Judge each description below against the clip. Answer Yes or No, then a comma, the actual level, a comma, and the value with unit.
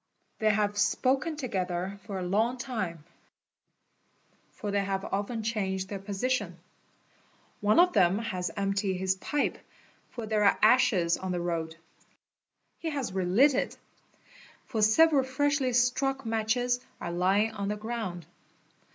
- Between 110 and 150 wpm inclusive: Yes, slow, 135 wpm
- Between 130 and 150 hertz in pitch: No, high, 210 Hz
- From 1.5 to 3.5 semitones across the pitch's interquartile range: No, average, 4.5 semitones